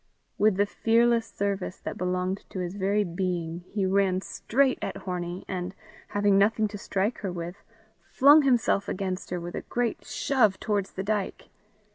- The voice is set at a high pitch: Yes, high, 195 Hz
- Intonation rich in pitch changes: No, average, 2.8 semitones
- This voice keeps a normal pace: Yes, average, 165 wpm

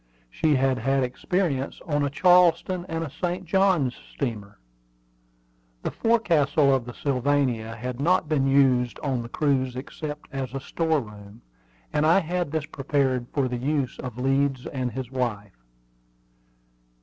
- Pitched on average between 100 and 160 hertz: Yes, low, 135 Hz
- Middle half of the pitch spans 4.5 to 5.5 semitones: No, average, 3.8 semitones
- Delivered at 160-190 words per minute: No, average, 150 wpm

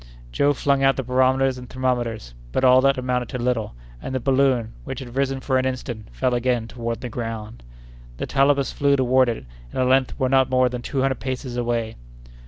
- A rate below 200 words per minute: No, fast, 205 wpm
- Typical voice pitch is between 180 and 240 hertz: No, low, 130 Hz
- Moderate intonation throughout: No, narrow, 1.8 semitones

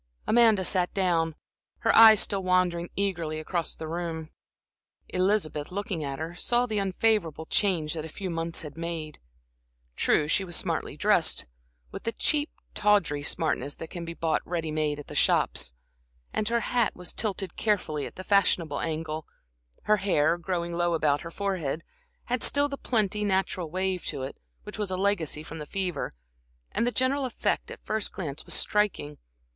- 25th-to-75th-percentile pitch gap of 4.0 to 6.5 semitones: Yes, average, 4.3 semitones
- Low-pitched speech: No, medium, 175 Hz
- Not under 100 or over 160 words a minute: No, average, 175 wpm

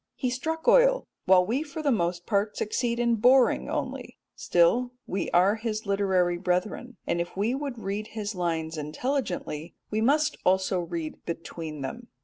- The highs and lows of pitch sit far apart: Yes, wide, 5.9 semitones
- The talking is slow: No, average, 160 wpm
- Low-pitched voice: No, high, 205 Hz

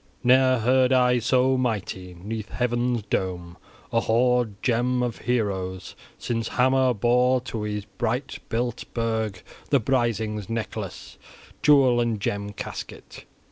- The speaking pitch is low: Yes, low, 120 Hz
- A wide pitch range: No, average, 2.9 semitones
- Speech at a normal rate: No, slow, 125 wpm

